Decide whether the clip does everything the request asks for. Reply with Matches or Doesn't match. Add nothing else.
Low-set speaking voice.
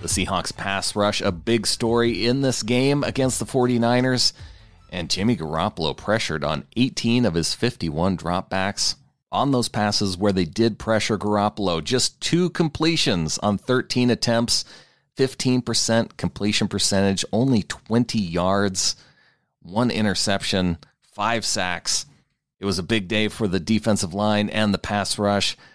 Matches